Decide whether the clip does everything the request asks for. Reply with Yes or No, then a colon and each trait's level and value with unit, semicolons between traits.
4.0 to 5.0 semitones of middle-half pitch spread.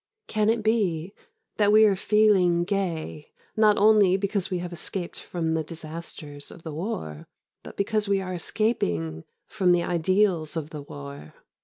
Yes: average, 4.5 semitones